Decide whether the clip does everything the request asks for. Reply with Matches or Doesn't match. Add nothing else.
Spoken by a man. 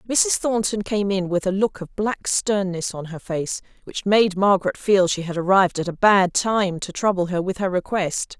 Doesn't match